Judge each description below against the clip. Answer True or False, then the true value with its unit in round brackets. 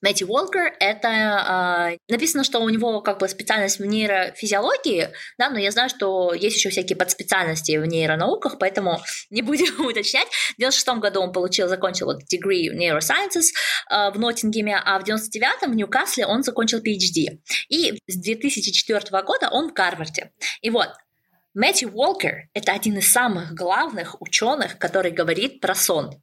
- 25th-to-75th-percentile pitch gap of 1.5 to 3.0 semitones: False (4.7 semitones)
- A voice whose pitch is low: False (210 Hz)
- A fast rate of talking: True (165 wpm)